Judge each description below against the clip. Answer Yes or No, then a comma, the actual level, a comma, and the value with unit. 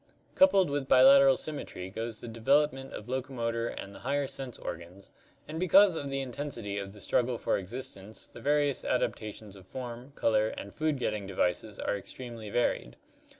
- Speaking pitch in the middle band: No, low, 120 Hz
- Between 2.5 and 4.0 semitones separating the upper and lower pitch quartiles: No, average, 4.7 semitones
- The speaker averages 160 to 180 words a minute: Yes, average, 170 wpm